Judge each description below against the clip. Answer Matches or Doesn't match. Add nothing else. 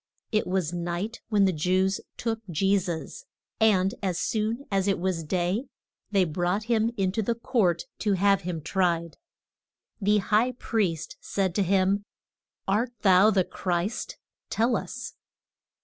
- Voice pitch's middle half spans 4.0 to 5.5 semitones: Doesn't match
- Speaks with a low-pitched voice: Doesn't match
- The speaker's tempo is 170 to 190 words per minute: Doesn't match